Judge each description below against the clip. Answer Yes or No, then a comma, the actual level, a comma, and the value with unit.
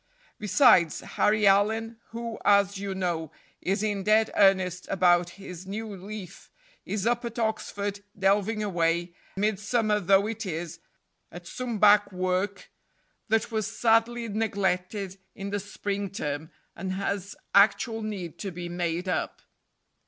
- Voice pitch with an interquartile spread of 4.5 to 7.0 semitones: No, average, 2.8 semitones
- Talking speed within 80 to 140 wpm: Yes, slow, 135 wpm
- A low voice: No, high, 200 Hz